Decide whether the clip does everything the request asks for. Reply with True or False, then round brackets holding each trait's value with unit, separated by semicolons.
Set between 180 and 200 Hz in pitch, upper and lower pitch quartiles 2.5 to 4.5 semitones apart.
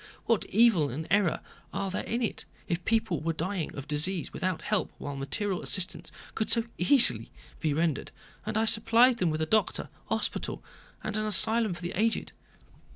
False (190 Hz; 5.1 semitones)